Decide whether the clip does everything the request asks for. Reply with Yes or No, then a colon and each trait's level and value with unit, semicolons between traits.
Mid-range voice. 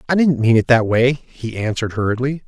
No: low, 125 Hz